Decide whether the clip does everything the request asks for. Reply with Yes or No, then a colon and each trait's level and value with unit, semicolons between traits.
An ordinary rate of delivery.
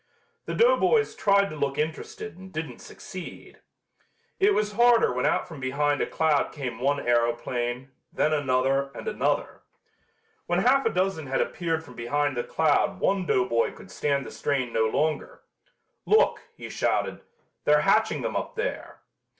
Yes: average, 160 wpm